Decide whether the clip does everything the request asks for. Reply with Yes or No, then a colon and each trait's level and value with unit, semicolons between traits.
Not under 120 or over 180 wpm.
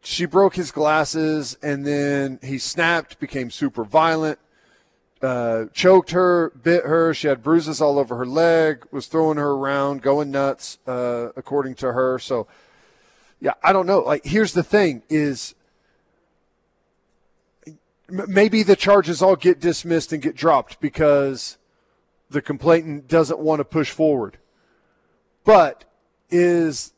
Yes: average, 140 wpm